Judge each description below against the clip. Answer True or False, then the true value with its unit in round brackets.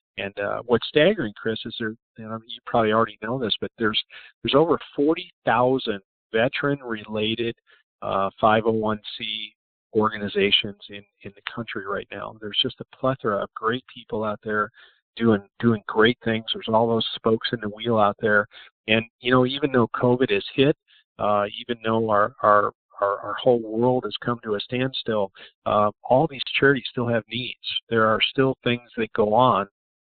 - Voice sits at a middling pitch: False (115 Hz)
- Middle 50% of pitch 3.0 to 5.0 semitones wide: False (2.6 semitones)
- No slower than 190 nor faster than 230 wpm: False (175 wpm)